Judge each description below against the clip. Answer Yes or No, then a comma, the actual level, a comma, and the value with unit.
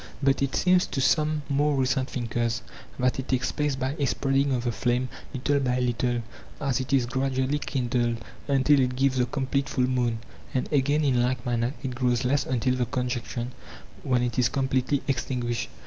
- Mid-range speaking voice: No, low, 130 Hz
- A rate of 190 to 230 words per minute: Yes, average, 195 wpm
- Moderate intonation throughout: No, narrow, 1.9 semitones